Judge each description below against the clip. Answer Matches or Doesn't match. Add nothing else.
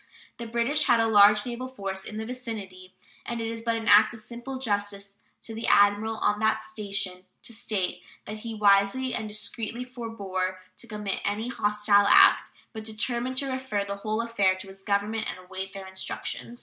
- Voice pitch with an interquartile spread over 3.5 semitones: Doesn't match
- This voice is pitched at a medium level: Doesn't match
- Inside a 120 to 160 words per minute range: Doesn't match